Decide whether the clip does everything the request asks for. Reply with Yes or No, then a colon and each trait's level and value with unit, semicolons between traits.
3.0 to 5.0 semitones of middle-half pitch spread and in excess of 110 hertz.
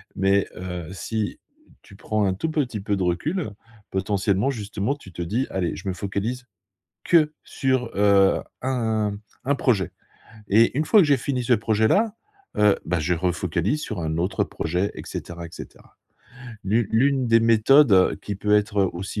No: average, 4.7 semitones; low, 105 Hz